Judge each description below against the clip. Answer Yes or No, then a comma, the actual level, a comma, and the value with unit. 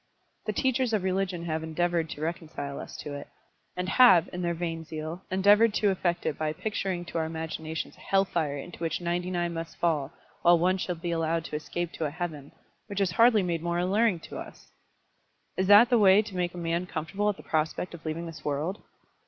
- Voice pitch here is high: No, medium, 175 Hz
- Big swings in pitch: No, average, 2.7 semitones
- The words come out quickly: Yes, fast, 215 wpm